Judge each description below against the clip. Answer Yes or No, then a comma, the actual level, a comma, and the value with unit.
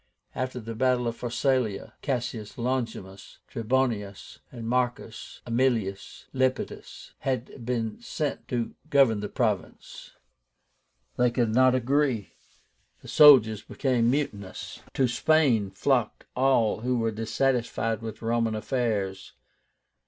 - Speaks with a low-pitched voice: Yes, low, 120 Hz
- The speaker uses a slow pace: Yes, slow, 110 wpm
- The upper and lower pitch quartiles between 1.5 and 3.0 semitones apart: Yes, average, 2.7 semitones